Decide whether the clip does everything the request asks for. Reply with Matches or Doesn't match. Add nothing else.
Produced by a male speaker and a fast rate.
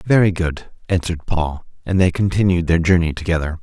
Doesn't match